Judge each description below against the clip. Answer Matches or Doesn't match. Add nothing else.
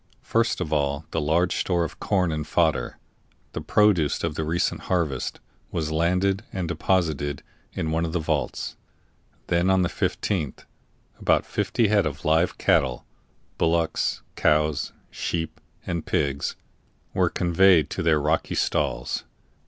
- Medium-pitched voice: Doesn't match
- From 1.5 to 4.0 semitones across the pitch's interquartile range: Matches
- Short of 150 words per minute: Matches